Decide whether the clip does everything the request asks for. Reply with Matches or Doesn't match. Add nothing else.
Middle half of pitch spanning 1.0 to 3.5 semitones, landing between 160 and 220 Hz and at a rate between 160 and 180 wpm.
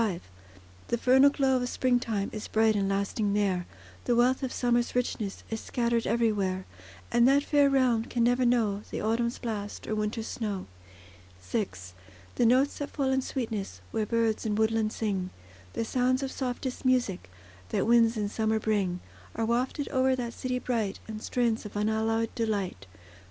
Doesn't match